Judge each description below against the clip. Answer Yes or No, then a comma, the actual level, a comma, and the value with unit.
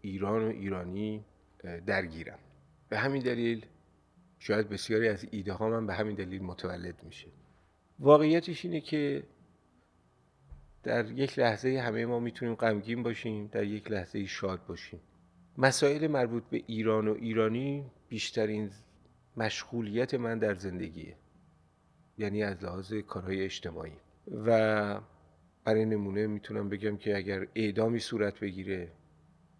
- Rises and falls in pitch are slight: No, average, 3.4 semitones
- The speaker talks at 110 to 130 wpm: Yes, average, 120 wpm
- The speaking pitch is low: Yes, low, 105 Hz